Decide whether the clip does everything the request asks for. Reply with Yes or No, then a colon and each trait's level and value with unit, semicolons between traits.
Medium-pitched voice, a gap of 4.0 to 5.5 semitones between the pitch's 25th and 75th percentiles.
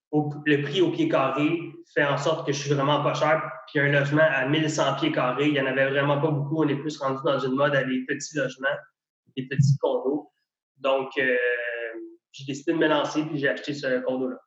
No: medium, 145 Hz; narrow, 2.4 semitones